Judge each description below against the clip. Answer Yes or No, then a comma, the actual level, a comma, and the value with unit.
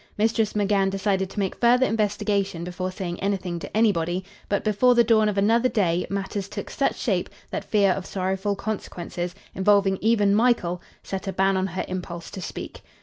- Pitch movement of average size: No, narrow, 2.2 semitones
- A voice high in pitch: Yes, high, 195 Hz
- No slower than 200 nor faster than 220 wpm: No, average, 180 wpm